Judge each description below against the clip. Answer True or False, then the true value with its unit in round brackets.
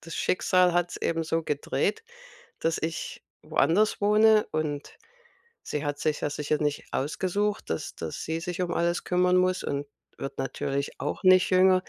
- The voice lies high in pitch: False (170 Hz)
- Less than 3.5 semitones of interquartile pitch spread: False (3.8 semitones)